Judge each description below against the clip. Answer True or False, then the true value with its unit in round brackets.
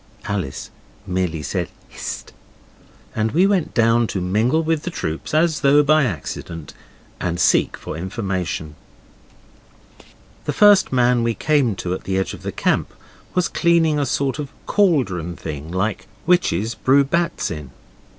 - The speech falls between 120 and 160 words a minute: True (150 wpm)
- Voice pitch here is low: True (115 Hz)